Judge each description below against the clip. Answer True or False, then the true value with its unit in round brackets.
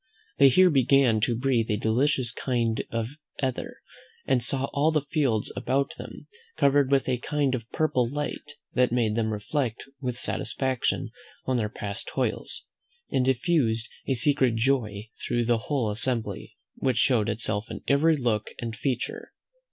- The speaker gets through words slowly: False (155 wpm)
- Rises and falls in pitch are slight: False (3.4 semitones)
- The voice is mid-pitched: False (125 Hz)